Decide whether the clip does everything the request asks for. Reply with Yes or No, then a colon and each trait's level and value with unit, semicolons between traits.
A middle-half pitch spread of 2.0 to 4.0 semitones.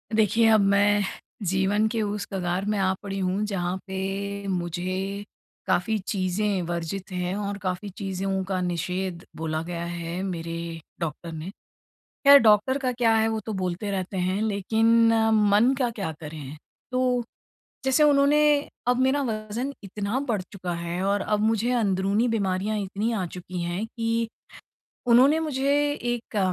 Yes: average, 3.4 semitones